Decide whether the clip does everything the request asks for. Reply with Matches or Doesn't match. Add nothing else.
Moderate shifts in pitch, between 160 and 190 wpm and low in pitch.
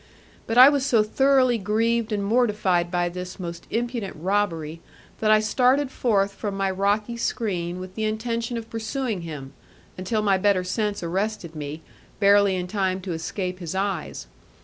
Doesn't match